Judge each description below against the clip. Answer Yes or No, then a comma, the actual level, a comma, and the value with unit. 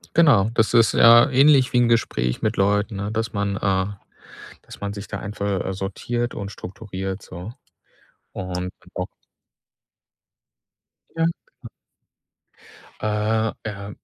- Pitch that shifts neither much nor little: Yes, average, 3.0 semitones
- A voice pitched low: Yes, low, 105 Hz